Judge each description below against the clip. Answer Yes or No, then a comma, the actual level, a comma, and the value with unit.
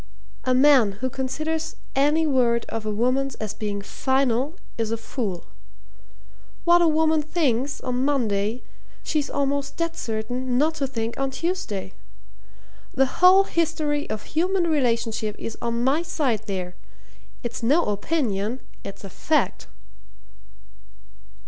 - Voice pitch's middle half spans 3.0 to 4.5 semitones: No, average, 5.2 semitones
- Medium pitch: No, very high, 260 Hz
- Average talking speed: No, slow, 130 wpm